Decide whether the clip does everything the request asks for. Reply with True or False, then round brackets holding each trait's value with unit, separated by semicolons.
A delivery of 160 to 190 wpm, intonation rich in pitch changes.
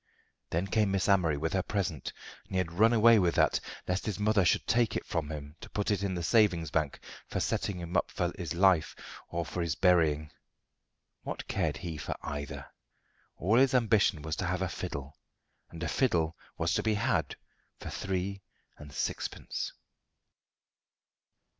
False (170 wpm; 3.9 semitones)